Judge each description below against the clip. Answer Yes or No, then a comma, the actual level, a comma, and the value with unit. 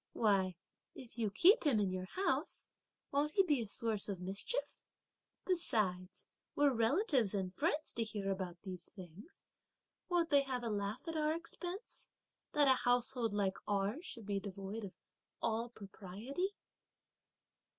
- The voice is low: No, high, 225 Hz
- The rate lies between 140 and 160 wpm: Yes, average, 150 wpm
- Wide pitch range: Yes, wide, 6.7 semitones